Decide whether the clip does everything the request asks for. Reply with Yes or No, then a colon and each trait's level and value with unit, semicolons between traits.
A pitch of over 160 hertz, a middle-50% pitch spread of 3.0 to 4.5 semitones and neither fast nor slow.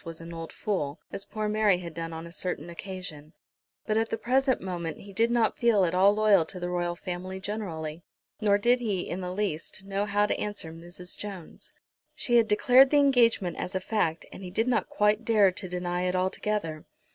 No: high, 190 Hz; average, 3.5 semitones; fast, 210 wpm